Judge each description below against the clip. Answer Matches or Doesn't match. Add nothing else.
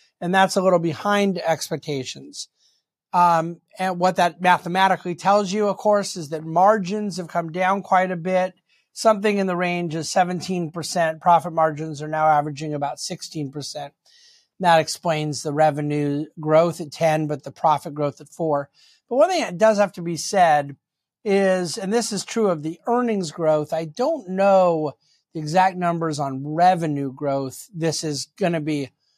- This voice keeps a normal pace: Matches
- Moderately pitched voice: Matches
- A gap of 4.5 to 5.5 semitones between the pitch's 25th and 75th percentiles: Doesn't match